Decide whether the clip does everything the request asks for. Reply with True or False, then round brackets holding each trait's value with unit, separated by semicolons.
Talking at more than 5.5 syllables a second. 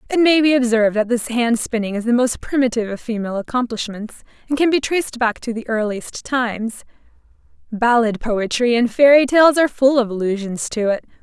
True (5.7 syllables/s)